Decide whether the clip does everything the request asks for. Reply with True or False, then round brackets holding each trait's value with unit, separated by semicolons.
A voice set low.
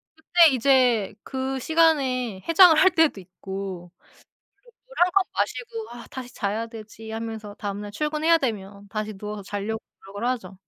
False (230 Hz)